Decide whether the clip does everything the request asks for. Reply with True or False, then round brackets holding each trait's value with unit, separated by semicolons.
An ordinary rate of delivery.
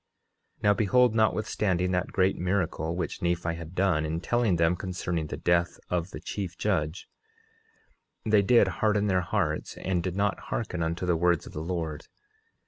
True (170 wpm)